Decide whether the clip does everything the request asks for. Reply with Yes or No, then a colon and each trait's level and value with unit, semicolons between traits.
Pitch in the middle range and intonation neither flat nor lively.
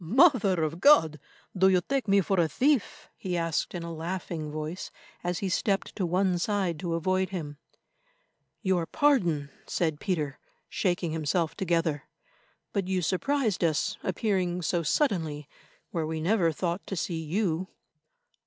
Yes: medium, 175 Hz; average, 3.2 semitones